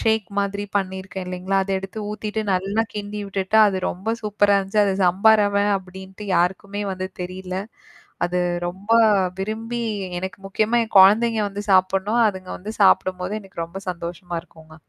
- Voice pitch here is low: No, high, 195 Hz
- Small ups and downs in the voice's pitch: Yes, narrow, 2.0 semitones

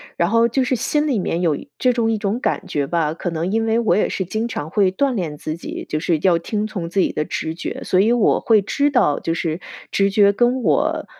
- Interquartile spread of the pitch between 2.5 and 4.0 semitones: No, wide, 5.5 semitones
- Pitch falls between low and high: No, high, 200 Hz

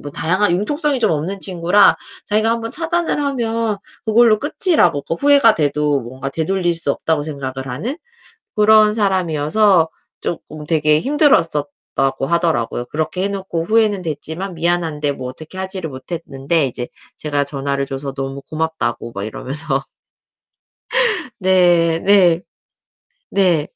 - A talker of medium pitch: Yes, medium, 165 Hz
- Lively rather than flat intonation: Yes, wide, 6.0 semitones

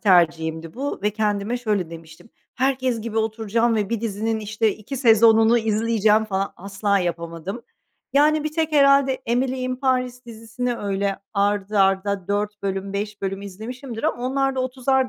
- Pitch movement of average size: Yes, average, 3.9 semitones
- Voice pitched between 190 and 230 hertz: Yes, high, 220 Hz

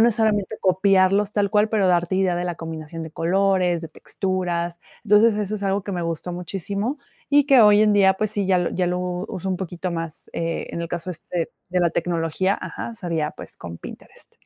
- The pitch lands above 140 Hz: Yes, medium, 185 Hz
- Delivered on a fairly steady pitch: No, average, 3.1 semitones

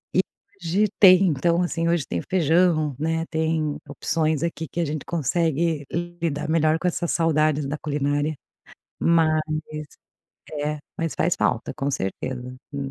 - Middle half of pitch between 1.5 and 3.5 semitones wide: Yes, narrow, 2.5 semitones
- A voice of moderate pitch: Yes, medium, 160 Hz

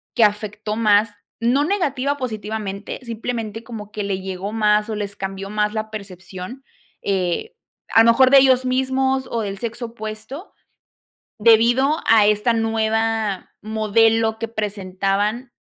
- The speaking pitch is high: Yes, high, 220 Hz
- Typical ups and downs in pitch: No, narrow, 2.3 semitones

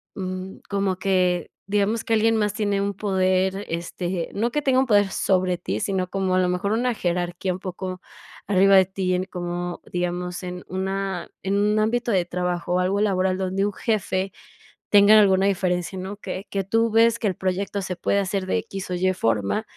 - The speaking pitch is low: No, high, 190 Hz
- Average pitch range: No, narrow, 1.8 semitones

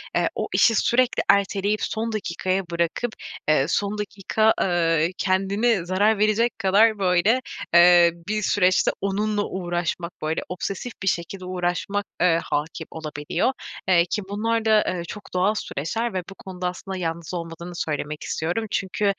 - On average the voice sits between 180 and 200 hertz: Yes, high, 190 Hz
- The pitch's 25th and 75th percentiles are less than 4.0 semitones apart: Yes, average, 3.5 semitones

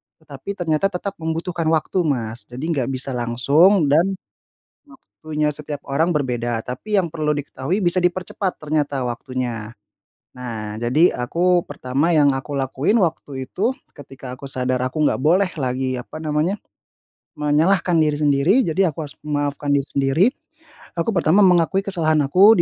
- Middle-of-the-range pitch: Yes, medium, 150 Hz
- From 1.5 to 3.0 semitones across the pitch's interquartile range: No, average, 4.6 semitones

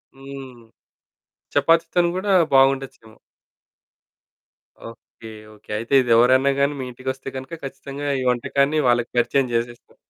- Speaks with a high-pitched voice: No, low, 135 Hz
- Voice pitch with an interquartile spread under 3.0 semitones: Yes, narrow, 2.4 semitones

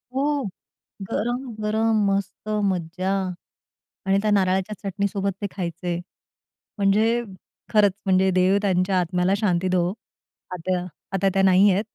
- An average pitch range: No, narrow, 2.0 semitones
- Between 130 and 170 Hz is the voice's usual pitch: No, high, 195 Hz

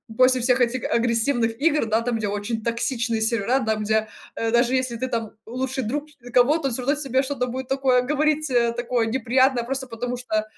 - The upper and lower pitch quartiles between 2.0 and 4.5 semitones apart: Yes, narrow, 2.5 semitones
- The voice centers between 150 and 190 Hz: No, high, 245 Hz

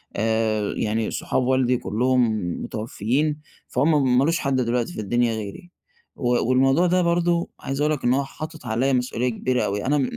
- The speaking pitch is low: Yes, low, 125 Hz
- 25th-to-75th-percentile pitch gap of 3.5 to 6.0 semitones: Yes, average, 4.1 semitones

